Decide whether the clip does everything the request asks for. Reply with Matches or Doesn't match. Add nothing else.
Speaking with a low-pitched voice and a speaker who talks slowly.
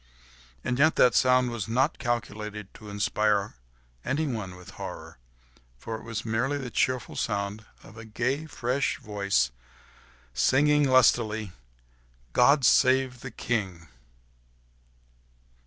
Matches